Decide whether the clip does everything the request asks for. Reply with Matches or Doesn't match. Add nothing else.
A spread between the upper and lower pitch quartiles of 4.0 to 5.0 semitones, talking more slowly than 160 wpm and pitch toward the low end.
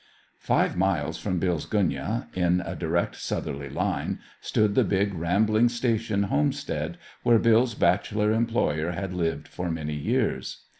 Matches